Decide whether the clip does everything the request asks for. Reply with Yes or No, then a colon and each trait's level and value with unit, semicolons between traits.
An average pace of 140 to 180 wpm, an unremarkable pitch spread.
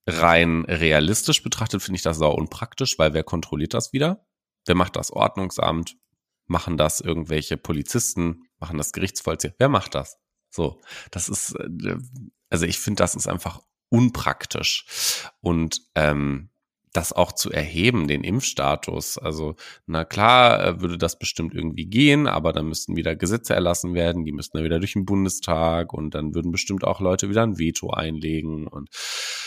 Yes: average, 155 wpm; average, 4.7 semitones